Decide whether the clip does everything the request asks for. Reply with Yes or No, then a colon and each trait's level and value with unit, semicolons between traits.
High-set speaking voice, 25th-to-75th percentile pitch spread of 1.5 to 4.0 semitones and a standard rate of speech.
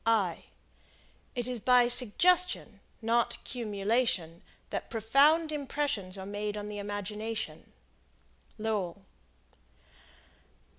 No: high, 220 Hz; average, 3.6 semitones; slow, 85 wpm